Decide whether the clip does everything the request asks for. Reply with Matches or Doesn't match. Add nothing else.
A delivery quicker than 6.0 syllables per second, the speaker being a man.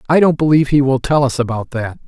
Matches